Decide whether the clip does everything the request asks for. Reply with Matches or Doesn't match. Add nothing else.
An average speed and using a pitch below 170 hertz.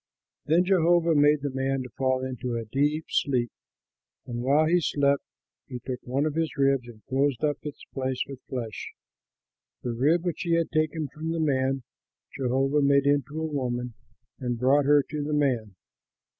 Matches